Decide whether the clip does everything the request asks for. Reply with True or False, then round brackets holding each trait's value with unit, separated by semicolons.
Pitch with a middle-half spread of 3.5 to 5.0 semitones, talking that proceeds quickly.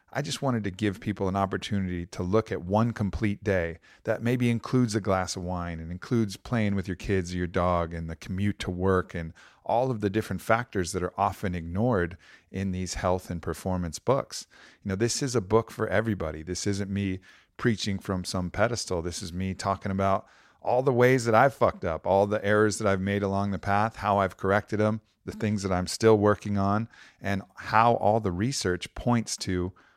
False (3.1 semitones; 210 wpm)